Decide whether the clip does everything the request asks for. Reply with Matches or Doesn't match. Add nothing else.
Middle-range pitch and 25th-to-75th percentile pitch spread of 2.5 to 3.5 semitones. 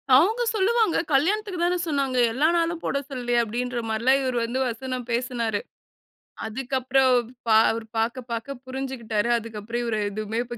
Doesn't match